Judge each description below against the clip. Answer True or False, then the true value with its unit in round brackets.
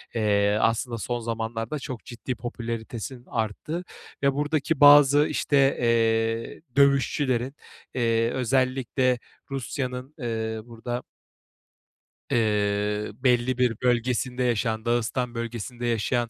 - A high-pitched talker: False (120 Hz)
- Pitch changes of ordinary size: False (2.3 semitones)